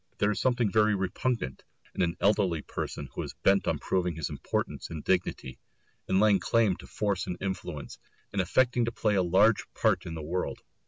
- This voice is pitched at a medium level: No, very low, 95 Hz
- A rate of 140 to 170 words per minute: No, average, 195 wpm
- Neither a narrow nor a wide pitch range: Yes, average, 3.3 semitones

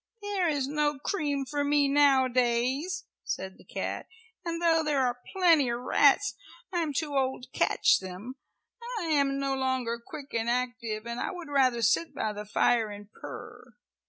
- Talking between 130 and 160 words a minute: No, average, 175 wpm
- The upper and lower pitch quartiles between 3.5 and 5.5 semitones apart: Yes, average, 3.9 semitones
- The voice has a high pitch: Yes, very high, 270 Hz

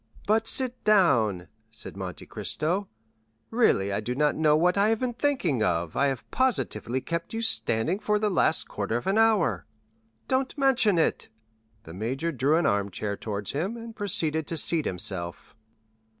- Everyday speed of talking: Yes, average, 165 wpm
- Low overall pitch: No, medium, 160 Hz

